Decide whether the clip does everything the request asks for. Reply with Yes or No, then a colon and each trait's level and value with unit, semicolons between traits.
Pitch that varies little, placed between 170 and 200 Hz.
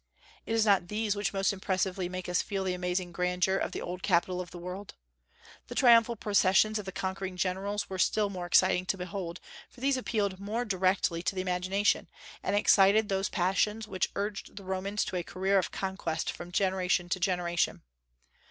Yes: narrow, 2.0 semitones; high, 190 Hz